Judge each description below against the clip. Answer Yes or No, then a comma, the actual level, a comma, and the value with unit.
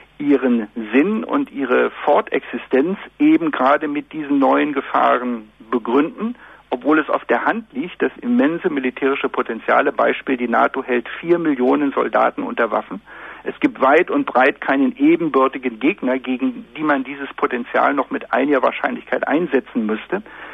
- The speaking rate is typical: Yes, average, 145 wpm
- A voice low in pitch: No, medium, 145 Hz